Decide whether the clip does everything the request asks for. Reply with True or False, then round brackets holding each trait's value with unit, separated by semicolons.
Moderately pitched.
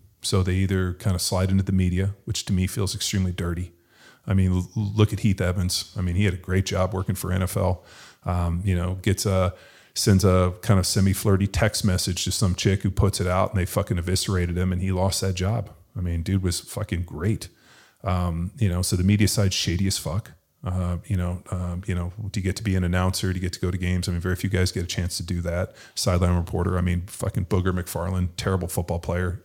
False (95 Hz)